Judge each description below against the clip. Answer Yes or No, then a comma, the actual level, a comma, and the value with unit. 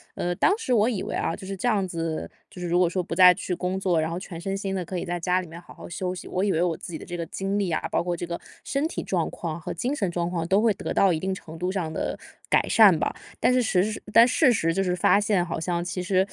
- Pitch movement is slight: Yes, narrow, 2.3 semitones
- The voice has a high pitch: No, medium, 180 Hz